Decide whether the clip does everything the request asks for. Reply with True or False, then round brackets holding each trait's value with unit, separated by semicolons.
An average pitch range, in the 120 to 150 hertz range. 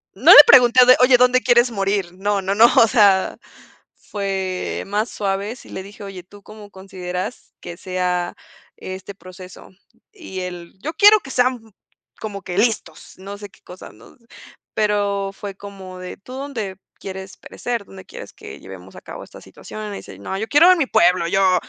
False (3.7 semitones; 200 Hz)